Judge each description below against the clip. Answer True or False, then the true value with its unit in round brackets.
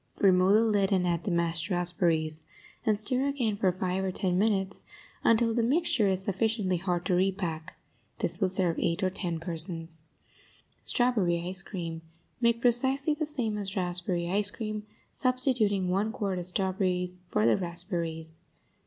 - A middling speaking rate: True (160 wpm)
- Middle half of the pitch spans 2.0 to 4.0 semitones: True (3.5 semitones)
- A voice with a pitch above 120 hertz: True (190 Hz)